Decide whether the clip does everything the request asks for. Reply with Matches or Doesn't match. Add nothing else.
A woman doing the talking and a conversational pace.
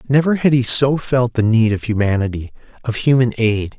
Doesn't match